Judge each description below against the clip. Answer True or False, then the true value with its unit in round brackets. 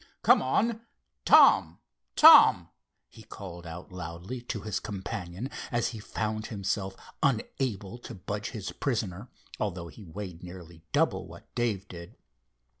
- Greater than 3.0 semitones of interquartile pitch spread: True (4.2 semitones)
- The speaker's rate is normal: False (130 wpm)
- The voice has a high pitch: False (100 Hz)